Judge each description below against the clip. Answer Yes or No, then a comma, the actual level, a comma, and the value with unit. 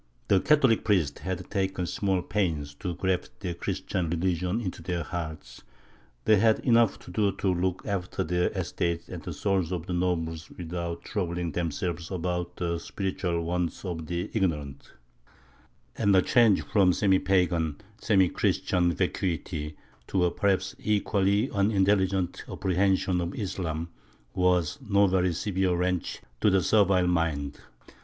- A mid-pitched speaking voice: No, very low, 90 Hz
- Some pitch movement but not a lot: No, narrow, 2.2 semitones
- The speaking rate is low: No, average, 145 wpm